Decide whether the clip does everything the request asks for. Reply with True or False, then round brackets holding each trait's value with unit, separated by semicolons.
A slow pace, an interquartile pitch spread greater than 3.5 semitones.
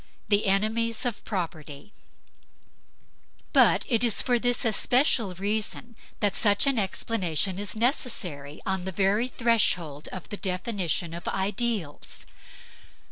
True (120 wpm; 4.1 semitones)